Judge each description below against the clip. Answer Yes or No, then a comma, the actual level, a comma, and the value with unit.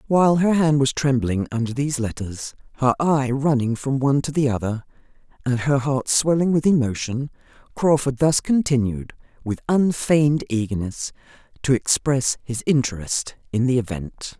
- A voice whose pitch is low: Yes, low, 130 Hz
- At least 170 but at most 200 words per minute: No, average, 145 wpm